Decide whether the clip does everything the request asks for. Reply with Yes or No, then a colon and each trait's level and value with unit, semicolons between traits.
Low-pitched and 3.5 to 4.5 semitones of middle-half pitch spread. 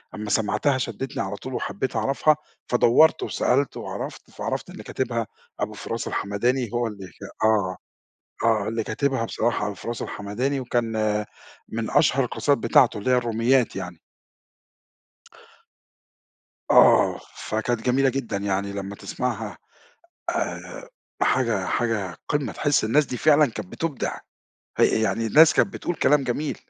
Yes: low, 115 Hz; average, 4.0 semitones